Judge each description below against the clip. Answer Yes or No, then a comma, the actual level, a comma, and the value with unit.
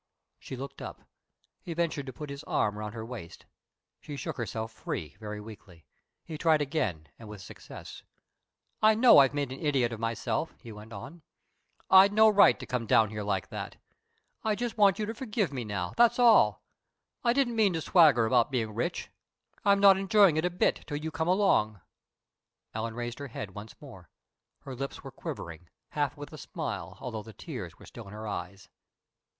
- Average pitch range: No, wide, 8.8 semitones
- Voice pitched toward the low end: Yes, low, 130 Hz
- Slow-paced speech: No, average, 190 wpm